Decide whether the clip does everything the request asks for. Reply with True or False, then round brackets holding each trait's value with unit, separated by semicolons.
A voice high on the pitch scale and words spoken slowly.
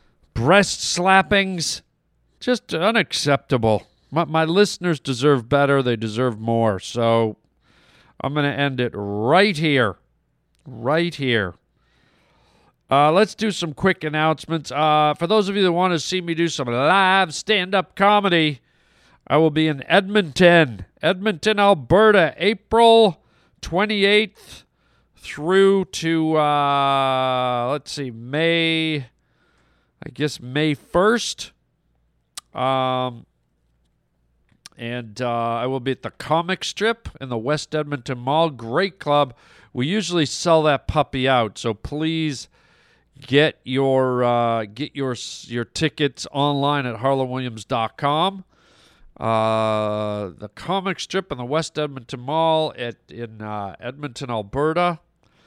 False (145 Hz; 120 wpm)